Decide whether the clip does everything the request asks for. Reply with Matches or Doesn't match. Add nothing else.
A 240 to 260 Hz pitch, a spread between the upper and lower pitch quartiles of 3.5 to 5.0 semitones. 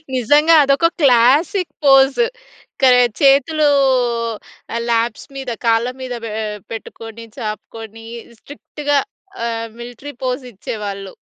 Matches